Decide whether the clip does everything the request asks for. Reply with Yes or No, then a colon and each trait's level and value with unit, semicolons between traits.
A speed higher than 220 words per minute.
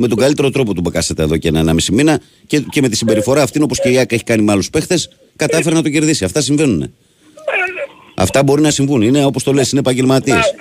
Yes: fast, 245 wpm